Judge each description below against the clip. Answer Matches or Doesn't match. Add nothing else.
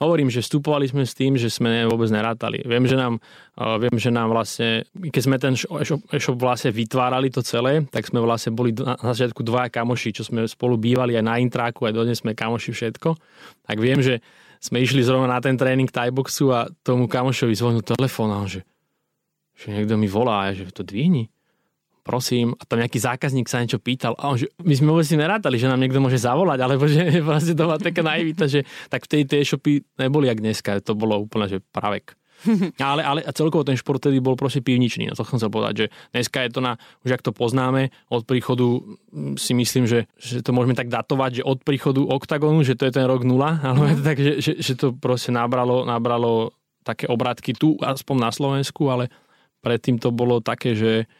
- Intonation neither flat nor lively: Matches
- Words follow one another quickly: Matches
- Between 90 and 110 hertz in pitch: Doesn't match